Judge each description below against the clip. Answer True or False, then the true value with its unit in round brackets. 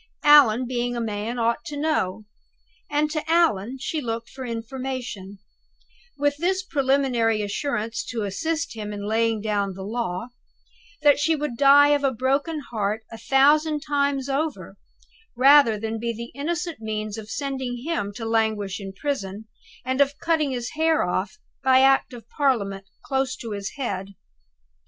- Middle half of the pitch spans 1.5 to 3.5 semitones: False (4.8 semitones)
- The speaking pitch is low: False (245 Hz)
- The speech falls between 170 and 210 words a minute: False (155 wpm)